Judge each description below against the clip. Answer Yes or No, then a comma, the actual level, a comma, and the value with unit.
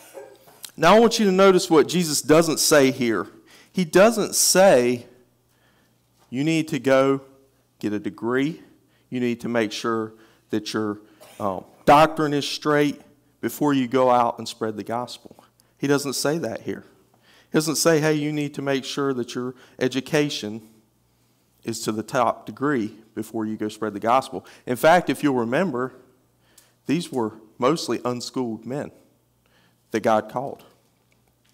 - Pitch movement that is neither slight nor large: Yes, average, 4.5 semitones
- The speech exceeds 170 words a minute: No, average, 155 wpm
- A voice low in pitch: Yes, low, 130 Hz